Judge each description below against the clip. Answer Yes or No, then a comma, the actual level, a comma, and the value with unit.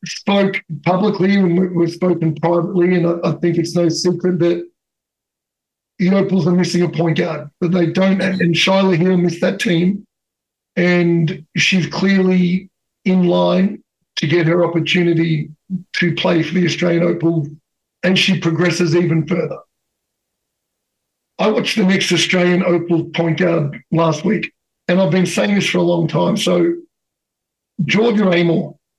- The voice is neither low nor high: Yes, medium, 175 Hz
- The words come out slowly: No, average, 150 wpm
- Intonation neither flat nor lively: No, narrow, 1.8 semitones